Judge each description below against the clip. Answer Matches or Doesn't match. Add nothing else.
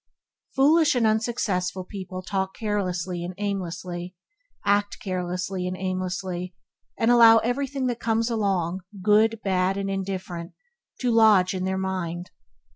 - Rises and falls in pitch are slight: Doesn't match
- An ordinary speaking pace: Doesn't match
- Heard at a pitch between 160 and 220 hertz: Matches